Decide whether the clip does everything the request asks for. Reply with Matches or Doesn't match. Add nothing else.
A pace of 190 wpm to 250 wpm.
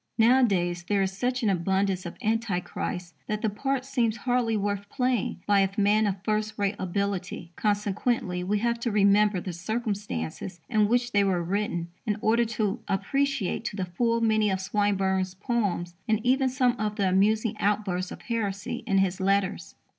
Doesn't match